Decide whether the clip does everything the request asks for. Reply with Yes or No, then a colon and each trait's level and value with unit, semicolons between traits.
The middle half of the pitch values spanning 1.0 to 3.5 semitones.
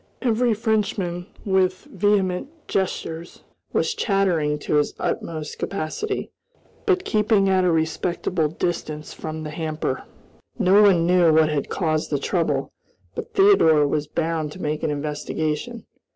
No: average, 4.2 semitones